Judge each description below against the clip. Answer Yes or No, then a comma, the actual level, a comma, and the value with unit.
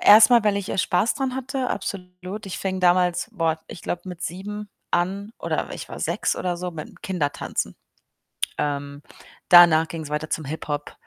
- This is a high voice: No, medium, 180 Hz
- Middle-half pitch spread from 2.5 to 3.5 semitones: No, average, 4.0 semitones